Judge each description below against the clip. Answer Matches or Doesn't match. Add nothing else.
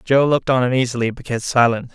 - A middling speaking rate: Doesn't match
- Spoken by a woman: Doesn't match